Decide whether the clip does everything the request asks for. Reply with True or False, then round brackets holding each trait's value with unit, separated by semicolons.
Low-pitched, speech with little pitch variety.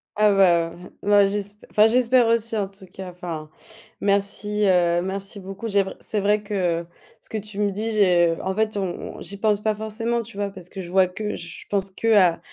False (200 Hz; 2.3 semitones)